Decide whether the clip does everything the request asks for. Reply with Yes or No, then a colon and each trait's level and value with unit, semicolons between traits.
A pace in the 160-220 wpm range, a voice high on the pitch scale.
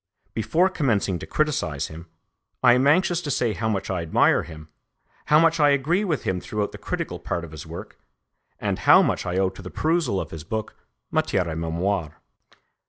No: average, 195 wpm; low, 105 Hz